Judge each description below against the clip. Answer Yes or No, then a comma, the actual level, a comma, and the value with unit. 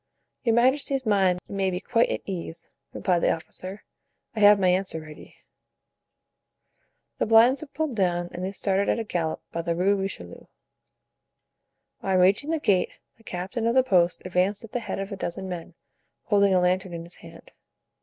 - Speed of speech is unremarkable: Yes, average, 180 wpm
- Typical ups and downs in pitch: Yes, average, 3.9 semitones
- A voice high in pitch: Yes, high, 195 Hz